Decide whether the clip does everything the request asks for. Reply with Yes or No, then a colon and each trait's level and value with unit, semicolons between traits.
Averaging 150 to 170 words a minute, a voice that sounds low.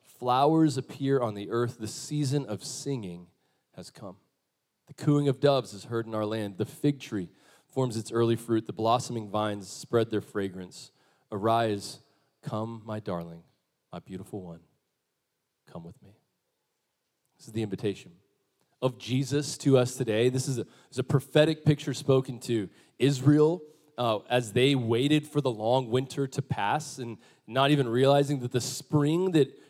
Yes: average, 165 wpm; low, 125 Hz